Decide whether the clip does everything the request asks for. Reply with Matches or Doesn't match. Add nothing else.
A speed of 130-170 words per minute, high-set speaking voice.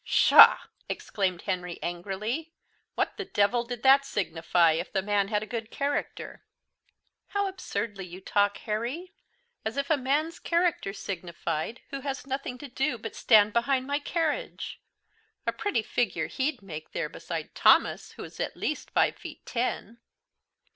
Matches